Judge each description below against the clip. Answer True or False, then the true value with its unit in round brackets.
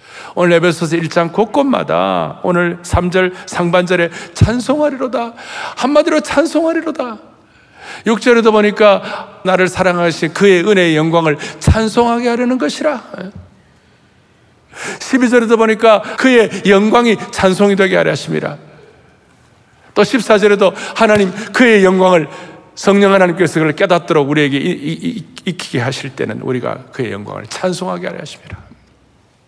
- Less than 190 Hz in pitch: False (200 Hz)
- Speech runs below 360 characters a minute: True (290 characters per minute)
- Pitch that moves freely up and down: False (5.0 semitones)